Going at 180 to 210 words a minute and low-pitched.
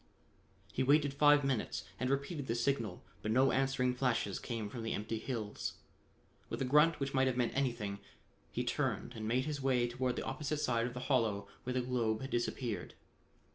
Yes: average, 190 wpm; low, 125 Hz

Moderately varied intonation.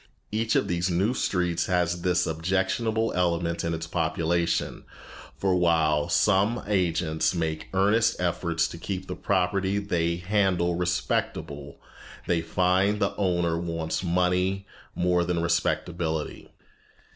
No: narrow, 2.2 semitones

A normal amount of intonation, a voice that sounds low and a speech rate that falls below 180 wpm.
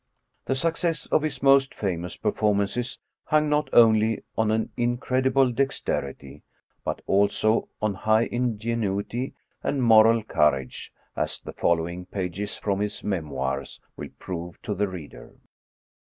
Yes: average, 4.9 semitones; low, 110 Hz; average, 140 wpm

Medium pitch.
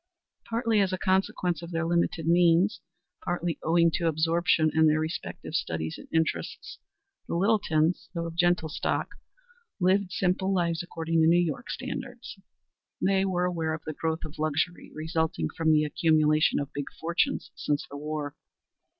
Yes: medium, 165 Hz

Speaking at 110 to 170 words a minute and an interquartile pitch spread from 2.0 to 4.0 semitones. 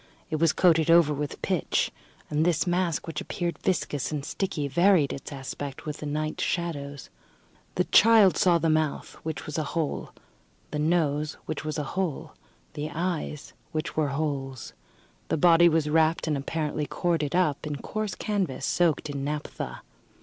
Yes: average, 165 wpm; average, 2.7 semitones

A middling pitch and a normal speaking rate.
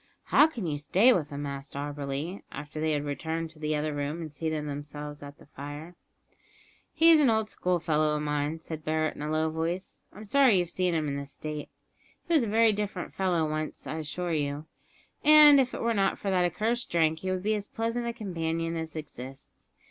No: medium, 160 Hz; fast, 215 wpm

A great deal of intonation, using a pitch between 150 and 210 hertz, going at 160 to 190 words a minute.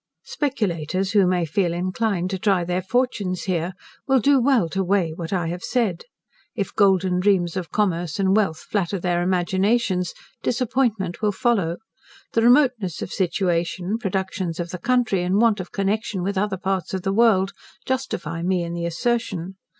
No: average, 3.4 semitones; high, 190 Hz; average, 165 wpm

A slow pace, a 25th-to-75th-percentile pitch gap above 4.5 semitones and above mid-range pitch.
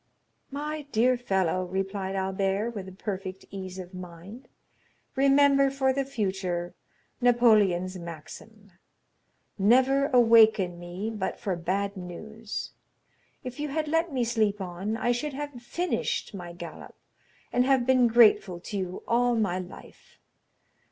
Yes: slow, 130 wpm; average, 5.0 semitones; high, 210 Hz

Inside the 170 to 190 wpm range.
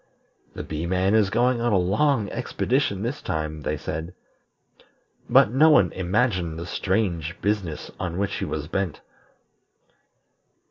No: average, 140 wpm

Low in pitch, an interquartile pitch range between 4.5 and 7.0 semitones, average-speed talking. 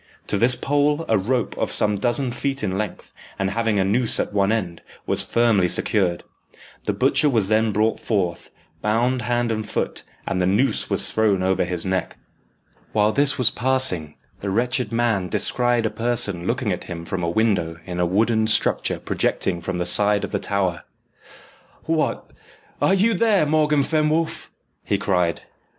Yes: low, 110 Hz; average, 4.8 semitones; average, 170 wpm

